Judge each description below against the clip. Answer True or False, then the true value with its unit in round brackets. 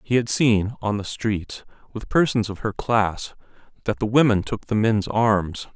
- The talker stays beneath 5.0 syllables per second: True (4.2 syllables/s)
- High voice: False (110 Hz)